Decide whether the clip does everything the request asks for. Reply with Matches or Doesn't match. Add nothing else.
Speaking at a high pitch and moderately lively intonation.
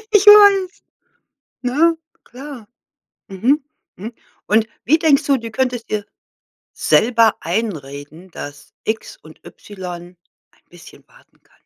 Doesn't match